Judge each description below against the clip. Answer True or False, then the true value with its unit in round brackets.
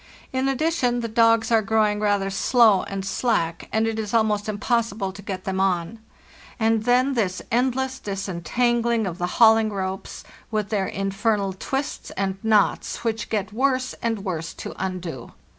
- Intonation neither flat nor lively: True (3.2 semitones)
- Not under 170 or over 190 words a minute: False (160 wpm)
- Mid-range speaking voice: False (215 Hz)